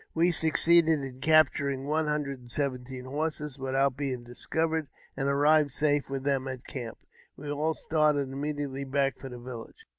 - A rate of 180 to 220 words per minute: No, average, 170 wpm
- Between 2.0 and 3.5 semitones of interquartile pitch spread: Yes, narrow, 2.4 semitones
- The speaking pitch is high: No, medium, 140 Hz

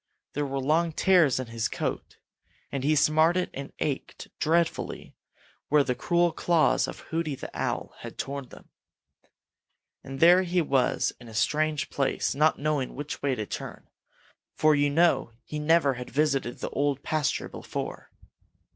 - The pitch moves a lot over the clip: No, average, 3.0 semitones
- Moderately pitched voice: Yes, medium, 145 Hz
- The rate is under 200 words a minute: Yes, average, 155 wpm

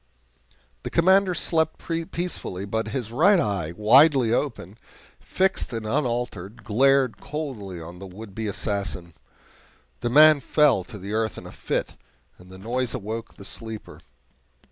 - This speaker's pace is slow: No, average, 145 wpm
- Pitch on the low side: Yes, low, 115 Hz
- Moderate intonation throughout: No, wide, 5.9 semitones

